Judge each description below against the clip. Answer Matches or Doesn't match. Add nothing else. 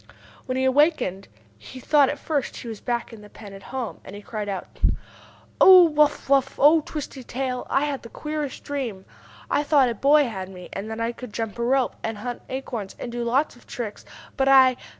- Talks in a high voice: Matches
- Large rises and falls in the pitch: Doesn't match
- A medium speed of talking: Doesn't match